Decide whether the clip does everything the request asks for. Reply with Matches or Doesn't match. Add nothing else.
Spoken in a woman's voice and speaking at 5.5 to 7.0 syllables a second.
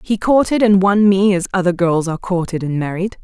Matches